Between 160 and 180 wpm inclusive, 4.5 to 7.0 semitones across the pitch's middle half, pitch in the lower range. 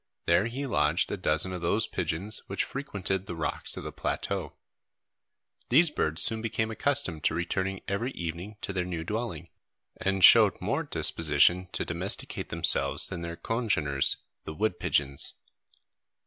No: average, 150 wpm; average, 5.1 semitones; very low, 90 Hz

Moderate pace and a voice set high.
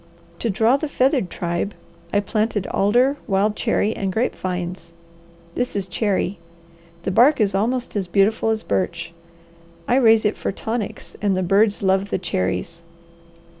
Yes: average, 155 wpm; high, 205 Hz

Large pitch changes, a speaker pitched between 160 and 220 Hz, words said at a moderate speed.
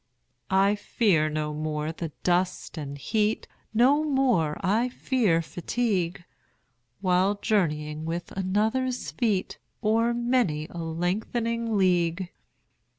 No: wide, 5.8 semitones; high, 190 Hz; slow, 110 wpm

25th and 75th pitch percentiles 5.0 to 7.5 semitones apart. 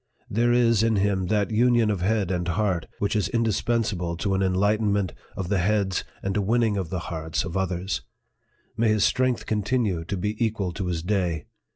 No: average, 3.2 semitones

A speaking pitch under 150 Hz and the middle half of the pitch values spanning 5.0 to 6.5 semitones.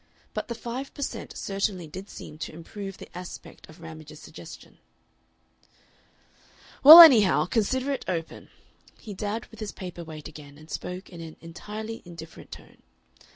No: medium, 185 Hz; average, 5.3 semitones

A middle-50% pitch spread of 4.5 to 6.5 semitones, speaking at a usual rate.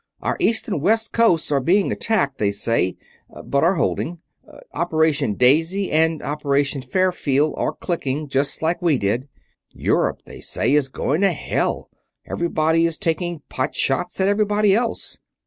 Yes: average, 5.0 semitones; average, 155 wpm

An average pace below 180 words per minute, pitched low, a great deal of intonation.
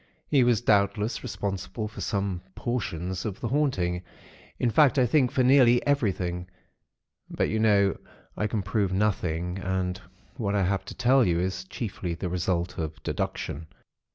No: average, 155 wpm; low, 100 Hz; average, 4.5 semitones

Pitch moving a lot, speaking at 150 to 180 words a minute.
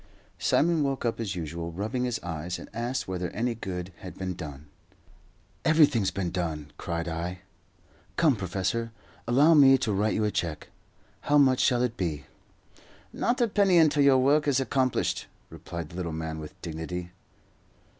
Yes: wide, 7.6 semitones; average, 165 wpm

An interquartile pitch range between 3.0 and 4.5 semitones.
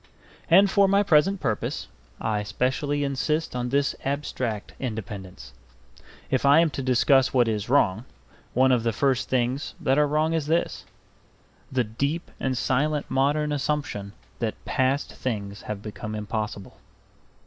No: average, 5.0 semitones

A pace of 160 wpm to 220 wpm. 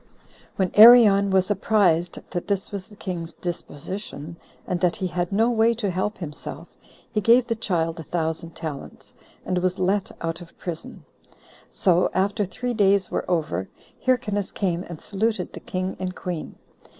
Yes: average, 165 wpm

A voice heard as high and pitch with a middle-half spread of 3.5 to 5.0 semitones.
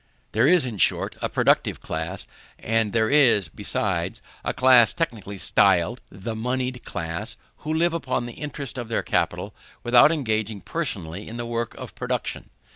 No: low, 115 Hz; average, 4.2 semitones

